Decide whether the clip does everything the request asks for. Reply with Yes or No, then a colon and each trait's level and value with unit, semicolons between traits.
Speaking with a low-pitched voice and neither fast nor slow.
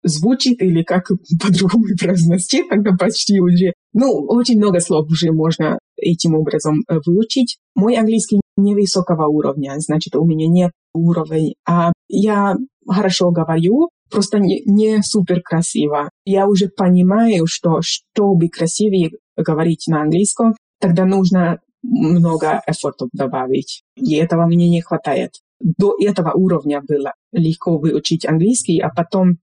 No: medium, 180 Hz; average, 130 wpm